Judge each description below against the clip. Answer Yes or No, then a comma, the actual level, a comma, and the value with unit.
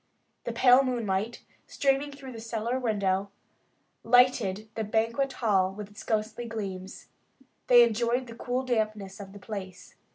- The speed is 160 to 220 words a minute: No, average, 140 wpm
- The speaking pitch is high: Yes, high, 225 Hz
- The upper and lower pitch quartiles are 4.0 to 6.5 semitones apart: No, average, 3.5 semitones